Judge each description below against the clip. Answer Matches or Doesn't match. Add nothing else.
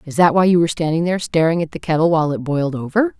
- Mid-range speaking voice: Matches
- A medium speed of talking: Doesn't match